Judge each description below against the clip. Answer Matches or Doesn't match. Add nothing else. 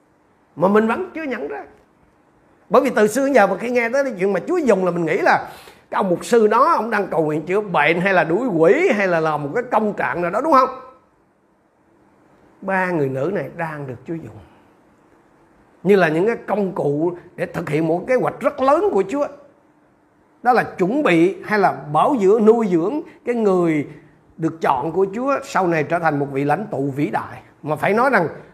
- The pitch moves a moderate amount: Doesn't match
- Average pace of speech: Matches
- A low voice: Doesn't match